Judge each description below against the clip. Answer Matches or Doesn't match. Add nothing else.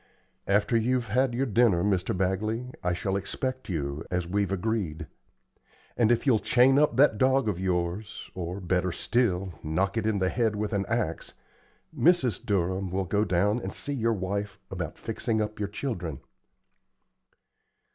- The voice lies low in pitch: Matches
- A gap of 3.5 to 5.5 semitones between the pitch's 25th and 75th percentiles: Matches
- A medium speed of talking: Matches